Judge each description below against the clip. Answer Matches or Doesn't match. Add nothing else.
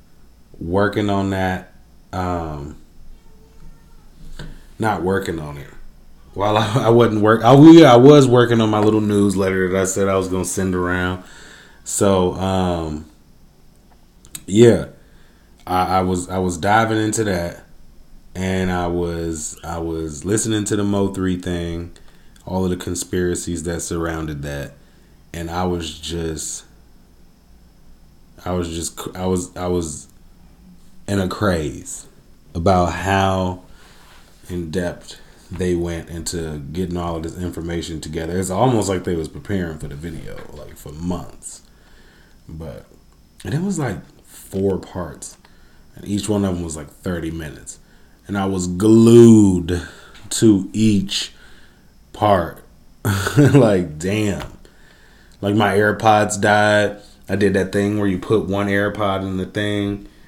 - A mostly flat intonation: Doesn't match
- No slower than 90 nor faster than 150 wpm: Matches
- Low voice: Matches